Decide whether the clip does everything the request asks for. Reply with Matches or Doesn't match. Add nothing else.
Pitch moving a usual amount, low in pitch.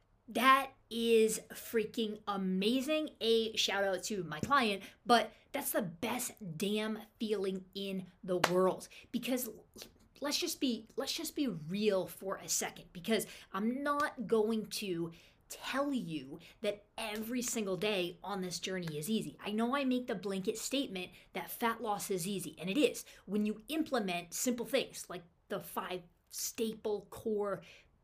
Doesn't match